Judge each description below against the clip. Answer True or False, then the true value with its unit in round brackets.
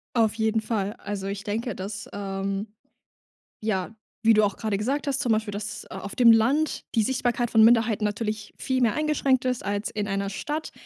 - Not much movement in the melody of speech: False (3.0 semitones)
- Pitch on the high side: True (220 Hz)